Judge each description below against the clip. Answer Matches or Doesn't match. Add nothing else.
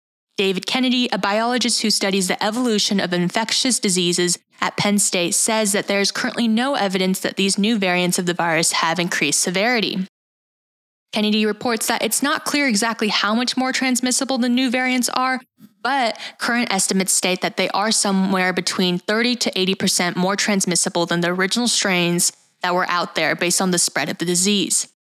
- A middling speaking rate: Matches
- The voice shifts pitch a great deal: Doesn't match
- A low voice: Doesn't match